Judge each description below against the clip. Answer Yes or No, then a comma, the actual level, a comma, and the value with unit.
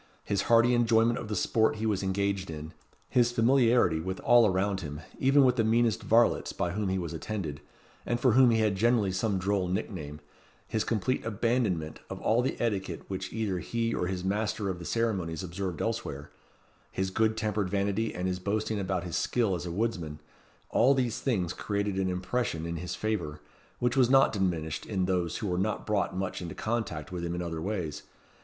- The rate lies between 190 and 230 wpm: Yes, average, 195 wpm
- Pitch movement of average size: Yes, average, 4.1 semitones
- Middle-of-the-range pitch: No, low, 100 Hz